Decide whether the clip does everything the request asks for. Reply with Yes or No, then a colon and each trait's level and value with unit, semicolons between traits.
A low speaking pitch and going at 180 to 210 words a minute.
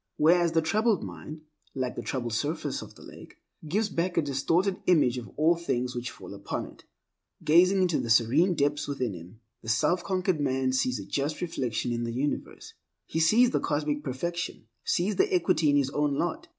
No: medium, 150 Hz; average, 190 wpm